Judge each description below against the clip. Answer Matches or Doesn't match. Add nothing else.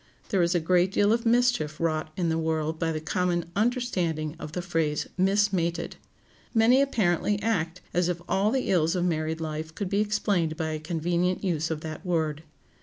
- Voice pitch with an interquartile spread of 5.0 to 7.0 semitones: Doesn't match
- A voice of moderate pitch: Matches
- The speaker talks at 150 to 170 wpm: Doesn't match